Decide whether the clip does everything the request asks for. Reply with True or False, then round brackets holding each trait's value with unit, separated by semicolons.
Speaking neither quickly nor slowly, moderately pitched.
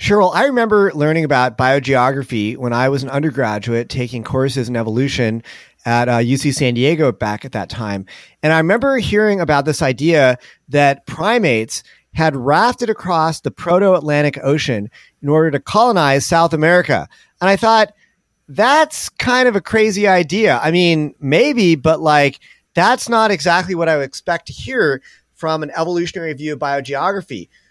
True (160 wpm; 150 Hz)